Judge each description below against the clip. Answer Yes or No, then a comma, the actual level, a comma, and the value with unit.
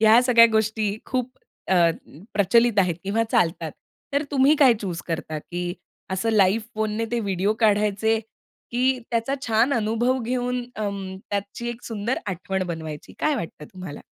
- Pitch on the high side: Yes, high, 220 Hz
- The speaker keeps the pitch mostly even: No, average, 3.8 semitones